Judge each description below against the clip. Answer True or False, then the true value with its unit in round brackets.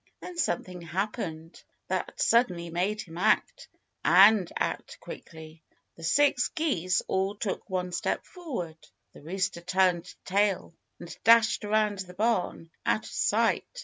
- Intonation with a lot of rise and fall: False (3.9 semitones)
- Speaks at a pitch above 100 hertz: True (190 Hz)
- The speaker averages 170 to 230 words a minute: False (135 wpm)